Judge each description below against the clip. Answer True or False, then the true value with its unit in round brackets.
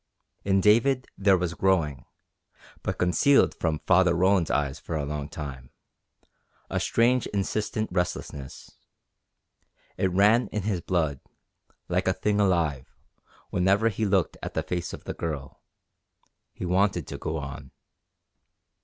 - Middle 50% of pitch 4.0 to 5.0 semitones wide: True (4.4 semitones)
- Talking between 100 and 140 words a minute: True (135 wpm)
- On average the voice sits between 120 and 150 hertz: False (90 Hz)